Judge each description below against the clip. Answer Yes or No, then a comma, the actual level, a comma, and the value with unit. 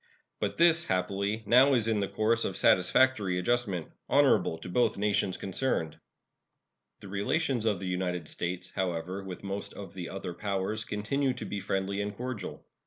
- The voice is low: Yes, low, 100 Hz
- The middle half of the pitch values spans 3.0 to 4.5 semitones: Yes, average, 3.7 semitones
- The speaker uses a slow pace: No, average, 165 wpm